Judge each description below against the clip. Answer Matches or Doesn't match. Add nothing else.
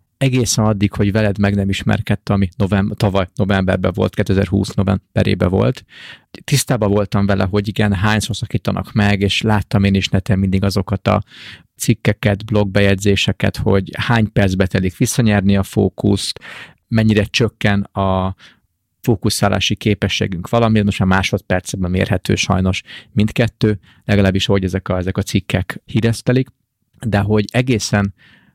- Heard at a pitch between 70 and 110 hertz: Matches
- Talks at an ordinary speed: Matches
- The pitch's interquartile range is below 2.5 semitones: Matches